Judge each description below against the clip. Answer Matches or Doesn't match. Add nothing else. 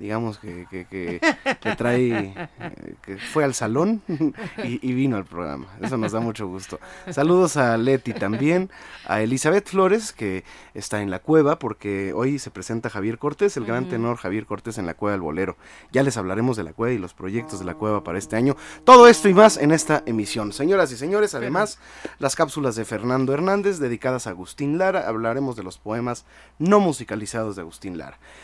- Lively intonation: Matches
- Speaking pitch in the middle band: Doesn't match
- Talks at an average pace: Doesn't match